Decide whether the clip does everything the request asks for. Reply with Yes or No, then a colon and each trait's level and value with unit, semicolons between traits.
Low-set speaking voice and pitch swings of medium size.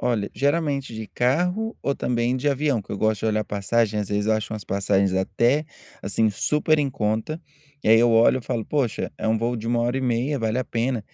Yes: low, 115 Hz; average, 3.7 semitones